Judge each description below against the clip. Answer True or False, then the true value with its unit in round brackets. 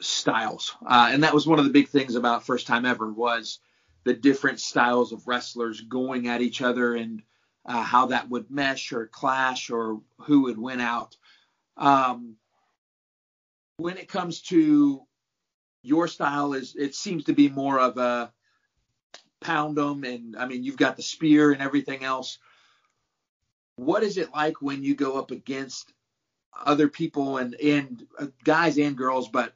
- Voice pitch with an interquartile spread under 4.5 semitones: True (3.1 semitones)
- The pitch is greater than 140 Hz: False (135 Hz)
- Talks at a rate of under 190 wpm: True (165 wpm)